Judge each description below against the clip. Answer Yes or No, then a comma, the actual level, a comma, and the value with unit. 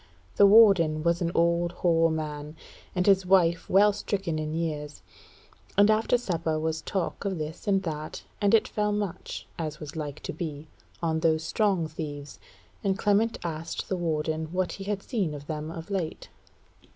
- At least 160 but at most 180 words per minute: Yes, average, 175 wpm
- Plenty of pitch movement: No, average, 3.8 semitones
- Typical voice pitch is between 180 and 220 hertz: No, medium, 170 Hz